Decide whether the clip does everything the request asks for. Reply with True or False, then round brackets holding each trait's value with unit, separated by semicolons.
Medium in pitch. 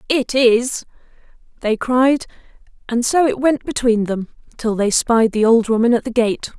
False (235 Hz)